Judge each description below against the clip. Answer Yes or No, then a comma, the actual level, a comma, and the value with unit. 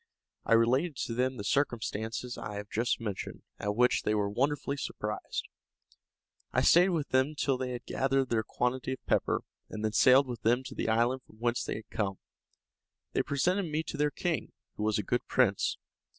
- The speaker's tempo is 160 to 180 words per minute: No, average, 195 wpm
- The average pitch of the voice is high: No, low, 125 Hz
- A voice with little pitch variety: No, average, 4.0 semitones